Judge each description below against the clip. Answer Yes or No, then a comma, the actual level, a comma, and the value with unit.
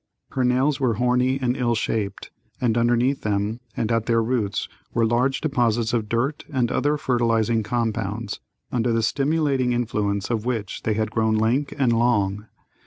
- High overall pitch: No, low, 120 Hz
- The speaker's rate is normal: Yes, average, 165 wpm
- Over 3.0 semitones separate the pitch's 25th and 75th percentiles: No, narrow, 2.4 semitones